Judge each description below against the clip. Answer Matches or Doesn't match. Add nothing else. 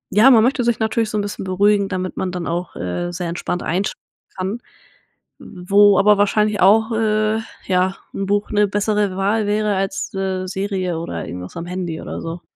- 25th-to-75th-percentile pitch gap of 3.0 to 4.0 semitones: Doesn't match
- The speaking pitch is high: Matches